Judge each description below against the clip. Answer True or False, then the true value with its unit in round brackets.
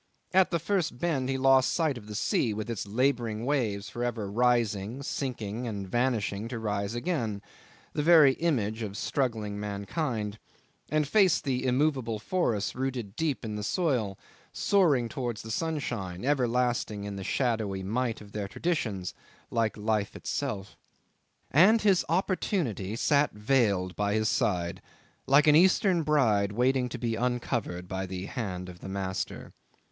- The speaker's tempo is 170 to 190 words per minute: False (150 wpm)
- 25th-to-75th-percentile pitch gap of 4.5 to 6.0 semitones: True (5.2 semitones)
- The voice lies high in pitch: False (120 Hz)